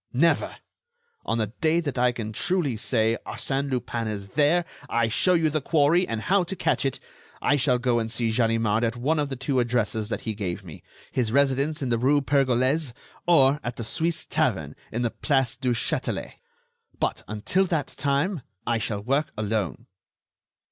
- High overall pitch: No, low, 125 Hz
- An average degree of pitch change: Yes, average, 4.4 semitones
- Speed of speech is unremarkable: Yes, average, 180 wpm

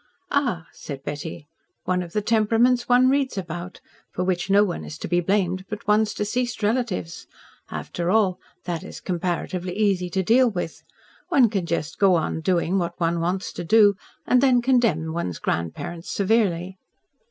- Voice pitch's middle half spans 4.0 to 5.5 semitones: Yes, average, 4.3 semitones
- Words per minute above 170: No, average, 165 wpm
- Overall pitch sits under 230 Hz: Yes, medium, 185 Hz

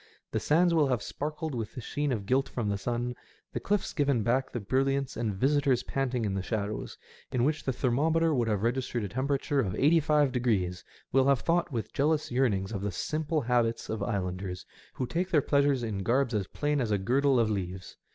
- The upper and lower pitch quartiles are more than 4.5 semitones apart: Yes, average, 4.9 semitones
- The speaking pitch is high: No, low, 125 Hz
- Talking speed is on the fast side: Yes, fast, 210 wpm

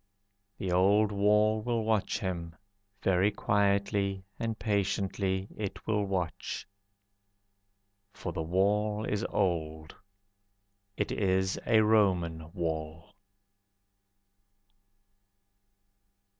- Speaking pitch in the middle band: No, low, 100 Hz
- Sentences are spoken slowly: Yes, slow, 85 wpm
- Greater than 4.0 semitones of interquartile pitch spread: No, average, 2.8 semitones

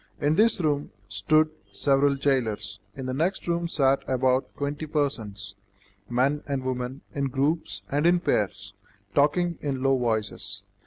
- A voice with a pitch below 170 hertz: Yes, low, 135 Hz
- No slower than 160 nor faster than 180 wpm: No, average, 145 wpm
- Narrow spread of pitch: No, average, 3.3 semitones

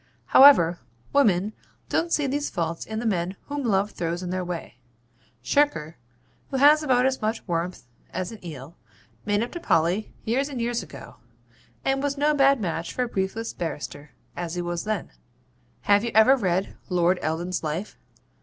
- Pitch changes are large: Yes, wide, 7.0 semitones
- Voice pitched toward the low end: No, high, 200 Hz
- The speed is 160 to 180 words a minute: Yes, average, 175 wpm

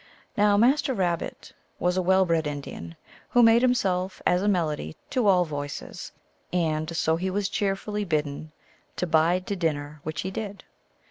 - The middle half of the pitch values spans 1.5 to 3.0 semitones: No, average, 4.4 semitones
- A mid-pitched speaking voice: Yes, medium, 180 Hz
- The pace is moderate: Yes, average, 170 wpm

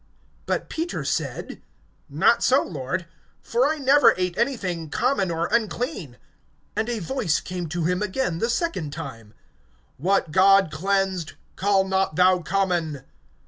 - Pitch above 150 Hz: Yes, high, 190 Hz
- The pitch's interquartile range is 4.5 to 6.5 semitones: Yes, average, 5.3 semitones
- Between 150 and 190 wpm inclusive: No, average, 140 wpm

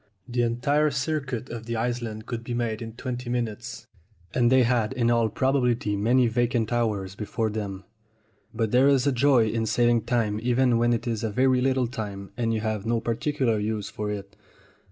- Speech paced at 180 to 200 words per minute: Yes, average, 190 wpm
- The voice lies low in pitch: Yes, low, 120 Hz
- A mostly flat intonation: Yes, narrow, 2.2 semitones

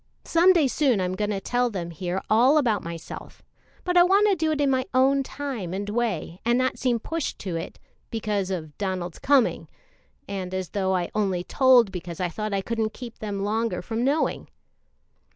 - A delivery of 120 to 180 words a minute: No, average, 195 wpm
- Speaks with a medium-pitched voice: No, high, 215 Hz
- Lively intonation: Yes, wide, 5.7 semitones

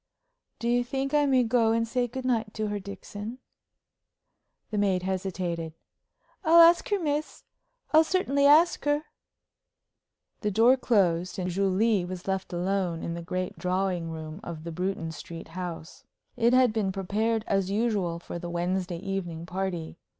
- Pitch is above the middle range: Yes, high, 195 Hz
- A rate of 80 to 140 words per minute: No, average, 155 wpm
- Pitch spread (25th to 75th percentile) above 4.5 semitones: Yes, average, 5.1 semitones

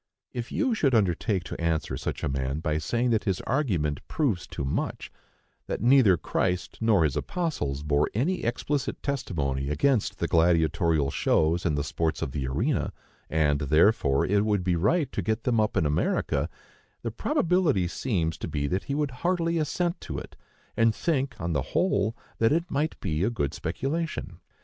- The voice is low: Yes, low, 100 Hz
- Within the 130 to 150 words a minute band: No, average, 175 wpm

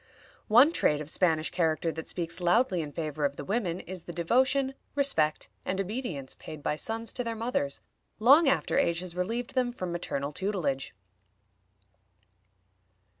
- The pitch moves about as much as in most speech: No, wide, 7.0 semitones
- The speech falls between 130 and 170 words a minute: Yes, average, 155 wpm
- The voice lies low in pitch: No, medium, 180 Hz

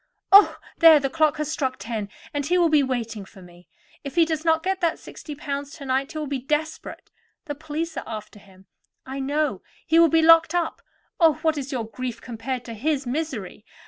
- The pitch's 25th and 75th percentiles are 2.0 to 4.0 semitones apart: No, average, 4.4 semitones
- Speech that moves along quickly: Yes, fast, 210 wpm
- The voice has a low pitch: No, very high, 285 Hz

